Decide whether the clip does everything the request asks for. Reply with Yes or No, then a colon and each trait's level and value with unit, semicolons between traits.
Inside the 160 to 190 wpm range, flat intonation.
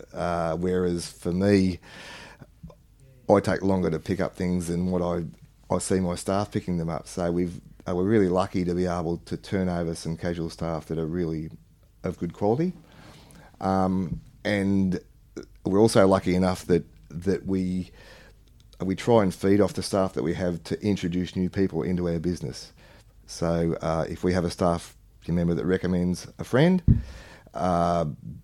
Yes: average, 170 wpm; narrow, 2.0 semitones